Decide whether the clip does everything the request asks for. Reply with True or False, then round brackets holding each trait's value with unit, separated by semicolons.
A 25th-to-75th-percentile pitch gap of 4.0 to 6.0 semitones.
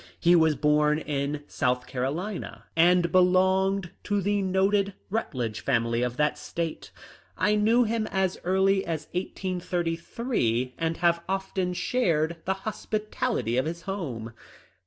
True (4.5 semitones)